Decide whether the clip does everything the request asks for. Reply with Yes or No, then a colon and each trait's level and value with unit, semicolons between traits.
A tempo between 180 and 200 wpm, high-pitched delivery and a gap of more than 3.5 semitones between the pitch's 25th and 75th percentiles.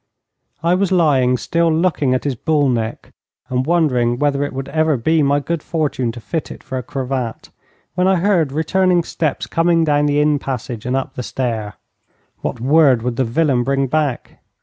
No: average, 190 wpm; medium, 140 Hz; average, 4.2 semitones